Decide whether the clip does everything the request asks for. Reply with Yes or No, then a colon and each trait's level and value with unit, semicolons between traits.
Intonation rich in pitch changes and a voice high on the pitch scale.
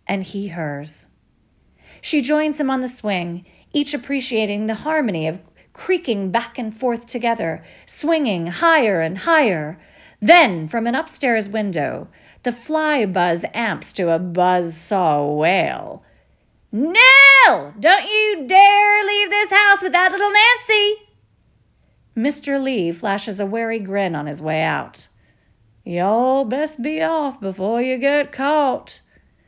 Yes: wide, 9.0 semitones; high, 235 Hz